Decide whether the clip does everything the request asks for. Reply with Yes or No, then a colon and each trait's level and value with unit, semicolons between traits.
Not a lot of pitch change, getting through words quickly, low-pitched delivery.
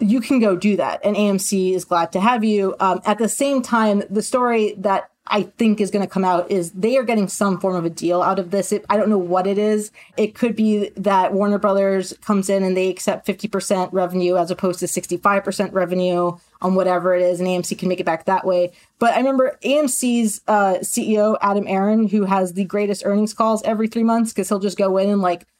No: narrow, 2.3 semitones; fast, 235 wpm; high, 200 Hz